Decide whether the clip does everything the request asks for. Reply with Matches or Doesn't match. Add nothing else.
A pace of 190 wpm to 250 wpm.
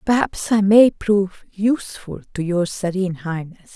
Doesn't match